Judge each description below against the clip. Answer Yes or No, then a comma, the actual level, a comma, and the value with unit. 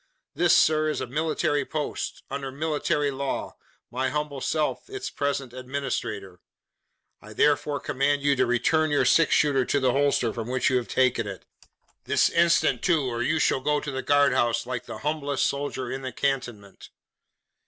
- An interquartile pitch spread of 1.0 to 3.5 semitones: Yes, average, 2.7 semitones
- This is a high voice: No, medium, 140 Hz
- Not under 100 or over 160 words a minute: No, average, 175 wpm